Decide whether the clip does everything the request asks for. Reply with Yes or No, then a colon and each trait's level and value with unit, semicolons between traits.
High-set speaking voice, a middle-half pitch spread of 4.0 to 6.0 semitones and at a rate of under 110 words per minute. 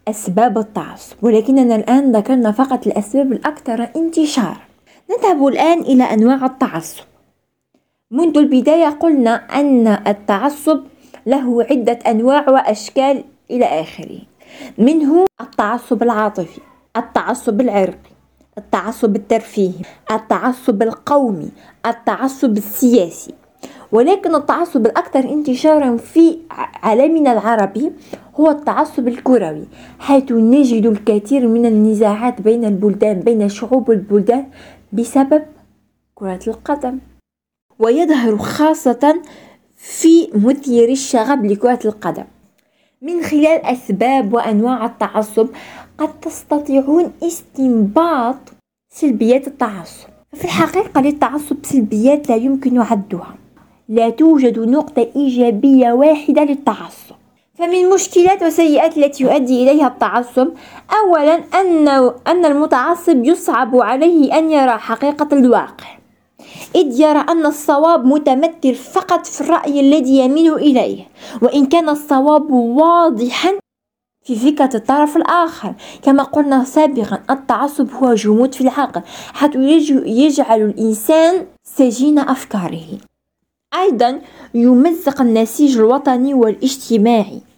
Yes: very high, 265 Hz; average, 4.4 semitones; average, 100 wpm